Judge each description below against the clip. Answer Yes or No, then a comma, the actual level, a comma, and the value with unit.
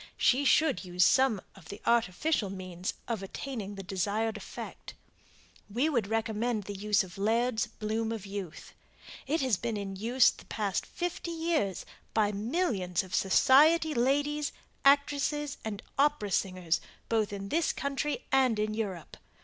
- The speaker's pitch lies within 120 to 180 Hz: No, high, 220 Hz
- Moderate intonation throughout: No, wide, 5.7 semitones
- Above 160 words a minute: No, average, 150 wpm